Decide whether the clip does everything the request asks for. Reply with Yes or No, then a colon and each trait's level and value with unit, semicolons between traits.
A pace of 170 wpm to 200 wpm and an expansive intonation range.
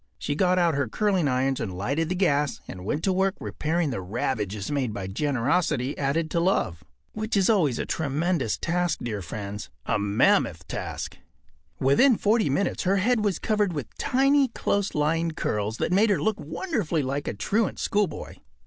Yes: average, 175 wpm; wide, 7.3 semitones